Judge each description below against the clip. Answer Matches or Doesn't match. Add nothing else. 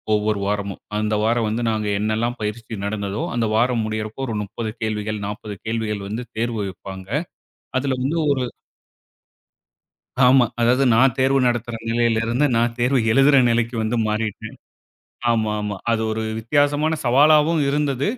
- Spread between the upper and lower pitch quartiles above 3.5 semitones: Doesn't match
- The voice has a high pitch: Doesn't match